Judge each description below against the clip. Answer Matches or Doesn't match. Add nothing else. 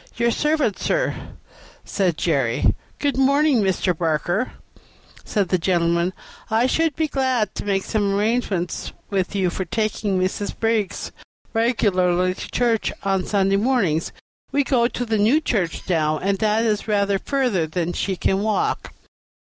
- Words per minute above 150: Doesn't match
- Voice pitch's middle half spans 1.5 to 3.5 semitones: Doesn't match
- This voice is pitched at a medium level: Doesn't match